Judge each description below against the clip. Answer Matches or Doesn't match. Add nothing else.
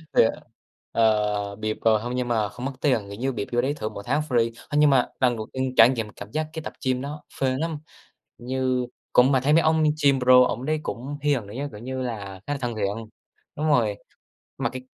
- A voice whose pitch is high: Doesn't match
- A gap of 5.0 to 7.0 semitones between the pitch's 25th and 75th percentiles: Doesn't match